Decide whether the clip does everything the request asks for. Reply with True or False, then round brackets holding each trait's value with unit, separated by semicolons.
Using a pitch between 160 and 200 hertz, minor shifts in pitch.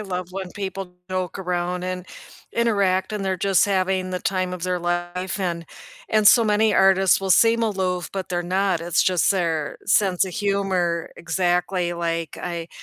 True (185 Hz; 1.8 semitones)